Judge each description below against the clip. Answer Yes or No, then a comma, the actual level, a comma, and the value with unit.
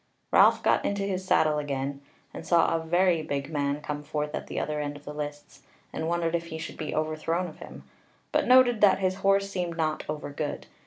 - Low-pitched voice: No, medium, 160 Hz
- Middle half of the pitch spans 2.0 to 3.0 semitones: No, average, 3.5 semitones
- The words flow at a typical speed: No, fast, 215 wpm